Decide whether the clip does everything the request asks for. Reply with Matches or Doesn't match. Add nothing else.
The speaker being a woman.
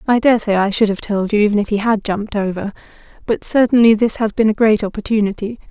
Matches